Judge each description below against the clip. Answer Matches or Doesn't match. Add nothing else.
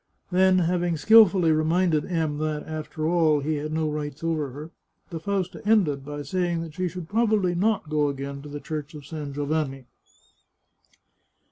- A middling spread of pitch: Matches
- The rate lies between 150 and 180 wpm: Matches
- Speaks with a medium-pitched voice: Matches